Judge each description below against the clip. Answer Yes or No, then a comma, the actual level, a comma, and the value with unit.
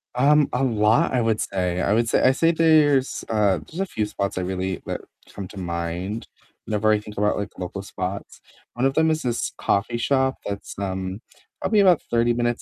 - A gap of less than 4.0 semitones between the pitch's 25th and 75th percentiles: No, average, 5.2 semitones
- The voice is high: No, low, 110 Hz